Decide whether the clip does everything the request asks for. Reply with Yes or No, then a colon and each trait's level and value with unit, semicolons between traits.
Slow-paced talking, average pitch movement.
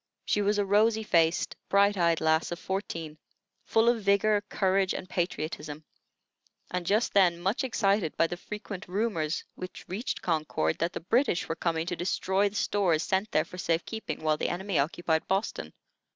No: average, 175 wpm; average, 3.6 semitones